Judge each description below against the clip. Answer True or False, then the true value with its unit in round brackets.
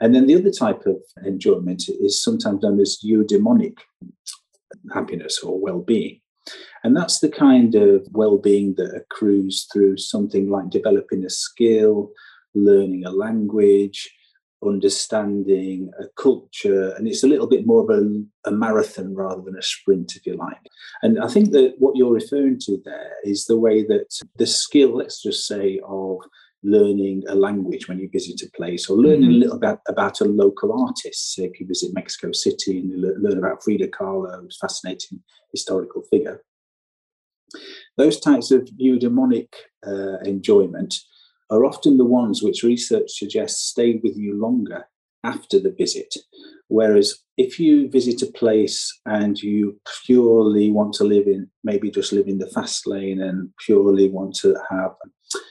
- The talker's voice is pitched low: True (110 Hz)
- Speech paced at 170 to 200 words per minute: False (160 wpm)